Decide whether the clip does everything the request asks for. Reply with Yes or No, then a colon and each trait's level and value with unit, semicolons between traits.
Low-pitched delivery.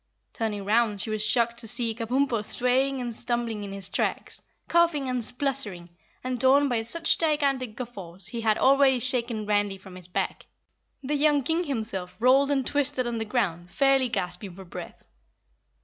No: high, 240 Hz